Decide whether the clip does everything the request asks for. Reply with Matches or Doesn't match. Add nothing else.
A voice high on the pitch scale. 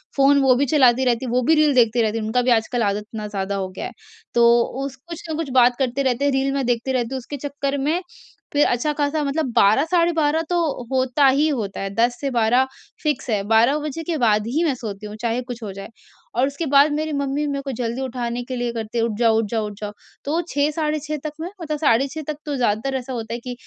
Matches